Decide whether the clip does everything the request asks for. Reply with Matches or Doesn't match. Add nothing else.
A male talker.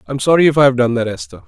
Matches